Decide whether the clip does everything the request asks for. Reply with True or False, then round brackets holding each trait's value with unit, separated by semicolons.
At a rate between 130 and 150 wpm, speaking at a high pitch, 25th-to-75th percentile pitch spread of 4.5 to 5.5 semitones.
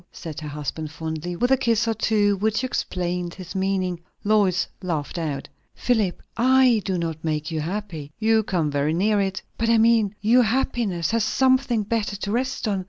False (180 wpm; 200 Hz; 5.1 semitones)